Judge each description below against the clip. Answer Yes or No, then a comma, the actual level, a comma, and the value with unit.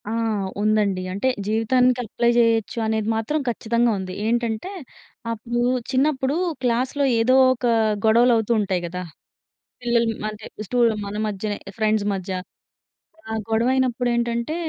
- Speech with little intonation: Yes, narrow, 2.3 semitones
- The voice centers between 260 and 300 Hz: No, high, 230 Hz